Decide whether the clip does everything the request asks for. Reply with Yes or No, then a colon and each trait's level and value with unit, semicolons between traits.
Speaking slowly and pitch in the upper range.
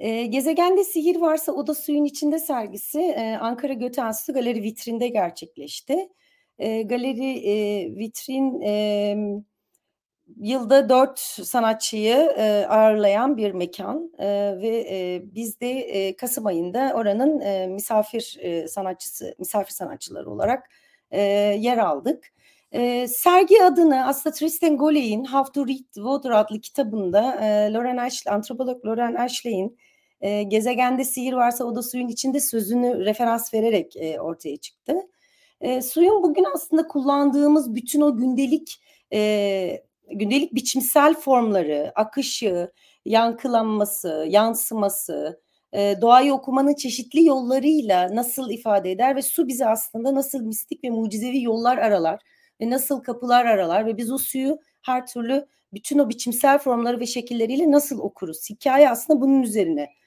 No: average, 120 wpm; high, 245 Hz